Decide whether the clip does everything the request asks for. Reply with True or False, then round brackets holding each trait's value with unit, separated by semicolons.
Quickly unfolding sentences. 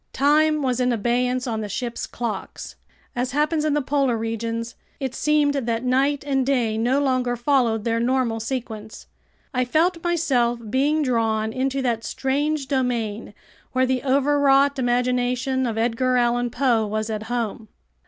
False (155 wpm)